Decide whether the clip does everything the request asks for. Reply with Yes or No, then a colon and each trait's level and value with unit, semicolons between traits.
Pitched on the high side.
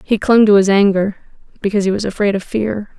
Yes: high, 205 Hz